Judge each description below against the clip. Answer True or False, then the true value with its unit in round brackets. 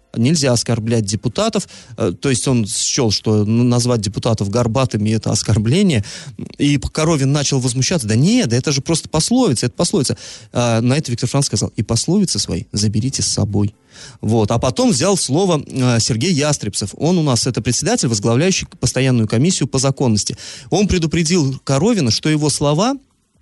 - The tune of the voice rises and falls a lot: False (4.6 semitones)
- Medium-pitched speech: False (125 Hz)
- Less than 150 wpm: False (155 wpm)